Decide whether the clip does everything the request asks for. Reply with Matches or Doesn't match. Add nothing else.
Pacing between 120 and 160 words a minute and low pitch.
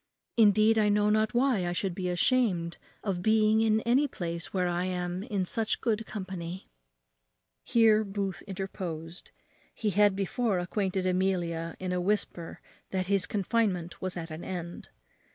Doesn't match